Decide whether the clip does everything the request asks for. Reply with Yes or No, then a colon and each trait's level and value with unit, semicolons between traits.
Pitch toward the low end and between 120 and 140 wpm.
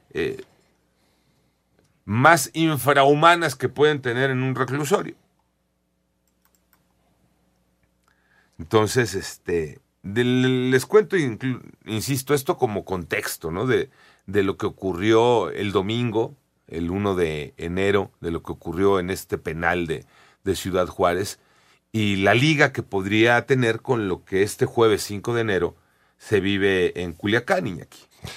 Yes: low, 110 Hz; average, 130 wpm